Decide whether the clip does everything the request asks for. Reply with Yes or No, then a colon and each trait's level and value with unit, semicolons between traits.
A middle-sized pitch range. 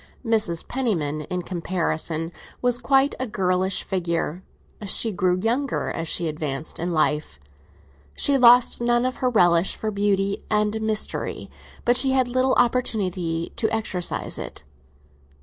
No: wide, 5.9 semitones